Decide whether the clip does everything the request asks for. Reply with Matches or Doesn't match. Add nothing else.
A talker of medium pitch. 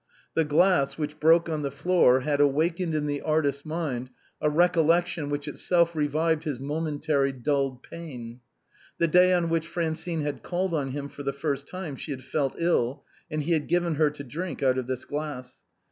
Matches